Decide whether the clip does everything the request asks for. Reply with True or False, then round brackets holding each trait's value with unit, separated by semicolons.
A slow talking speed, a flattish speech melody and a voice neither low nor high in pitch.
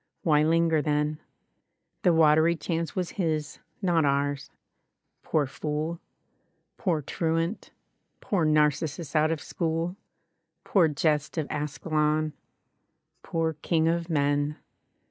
True (105 wpm; 1.8 semitones; 155 Hz)